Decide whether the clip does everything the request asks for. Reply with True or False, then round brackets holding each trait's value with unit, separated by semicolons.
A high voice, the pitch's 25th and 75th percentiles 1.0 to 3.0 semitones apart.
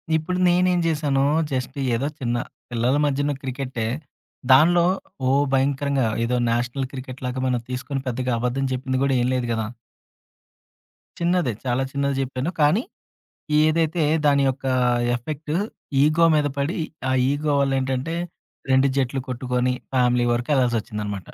False (135 Hz; 2.7 semitones)